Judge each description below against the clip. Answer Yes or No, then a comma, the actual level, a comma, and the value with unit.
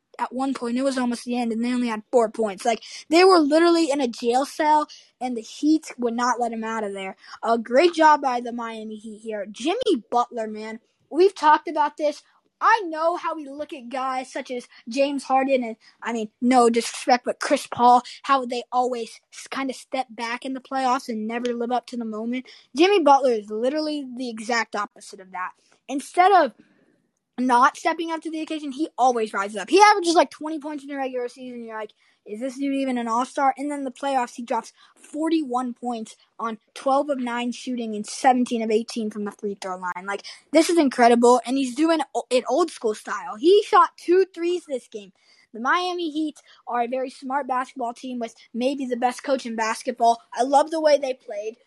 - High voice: Yes, very high, 255 Hz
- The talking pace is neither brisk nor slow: No, fast, 215 wpm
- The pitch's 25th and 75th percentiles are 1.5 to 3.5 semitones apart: No, average, 4.1 semitones